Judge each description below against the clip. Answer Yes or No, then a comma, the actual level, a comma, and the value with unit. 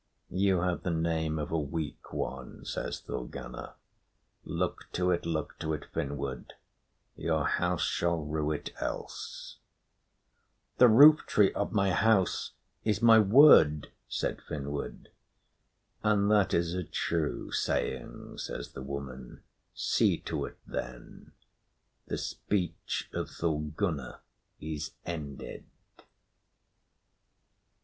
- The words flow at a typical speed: No, slow, 110 wpm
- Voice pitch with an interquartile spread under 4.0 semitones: No, average, 4.5 semitones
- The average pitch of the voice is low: Yes, very low, 80 Hz